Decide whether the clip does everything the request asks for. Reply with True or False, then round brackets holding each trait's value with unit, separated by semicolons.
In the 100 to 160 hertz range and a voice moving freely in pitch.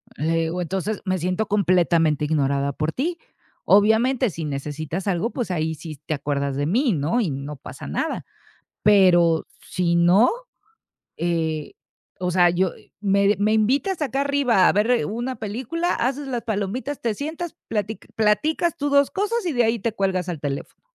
False (195 Hz; 6.9 semitones)